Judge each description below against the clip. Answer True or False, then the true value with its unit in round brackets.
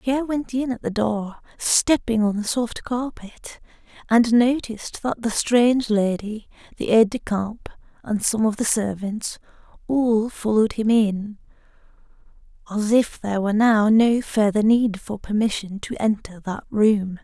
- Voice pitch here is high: True (220 Hz)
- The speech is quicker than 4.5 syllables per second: False (4.4 syllables/s)